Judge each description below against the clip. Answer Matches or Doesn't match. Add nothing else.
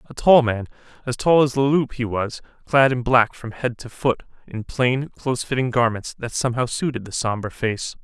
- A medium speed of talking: Doesn't match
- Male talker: Matches